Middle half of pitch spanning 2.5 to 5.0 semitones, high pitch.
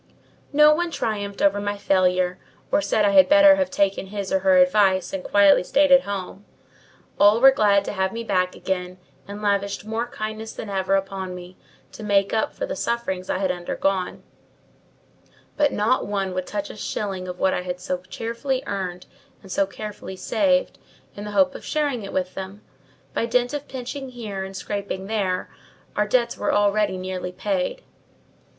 Yes: average, 3.6 semitones; high, 200 Hz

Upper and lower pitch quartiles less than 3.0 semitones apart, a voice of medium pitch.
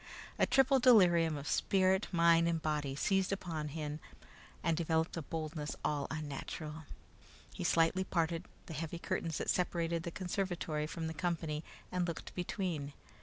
Yes: narrow, 2.5 semitones; medium, 165 Hz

